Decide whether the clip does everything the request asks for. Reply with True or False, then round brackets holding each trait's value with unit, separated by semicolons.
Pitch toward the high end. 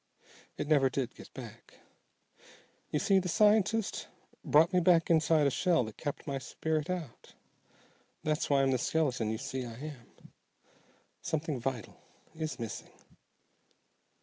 False (150 Hz)